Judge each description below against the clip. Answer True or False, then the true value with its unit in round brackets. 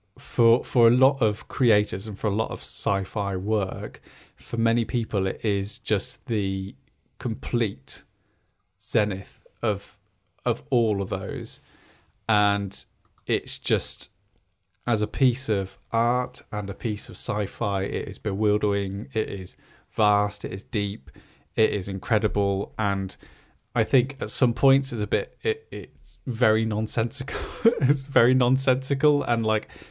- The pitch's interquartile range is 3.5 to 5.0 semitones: False (3.1 semitones)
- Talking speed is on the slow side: False (145 wpm)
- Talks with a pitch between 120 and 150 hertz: False (105 Hz)